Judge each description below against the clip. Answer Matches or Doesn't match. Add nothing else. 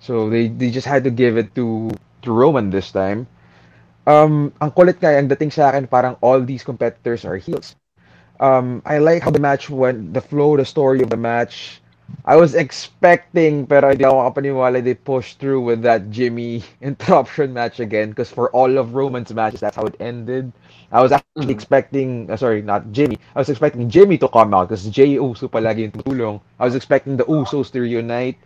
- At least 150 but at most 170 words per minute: Doesn't match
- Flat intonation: Doesn't match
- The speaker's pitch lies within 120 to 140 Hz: Matches